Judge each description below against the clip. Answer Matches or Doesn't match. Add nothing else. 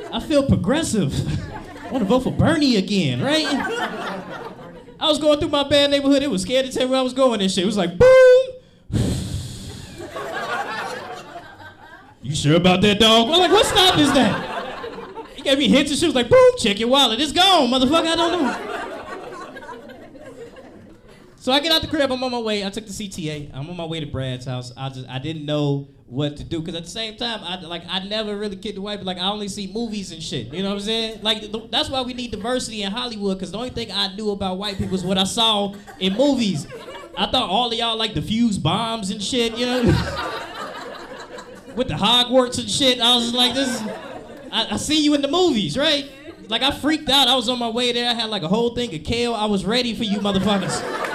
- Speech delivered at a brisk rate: Matches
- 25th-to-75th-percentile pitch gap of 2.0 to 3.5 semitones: Doesn't match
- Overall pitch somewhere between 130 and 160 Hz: Doesn't match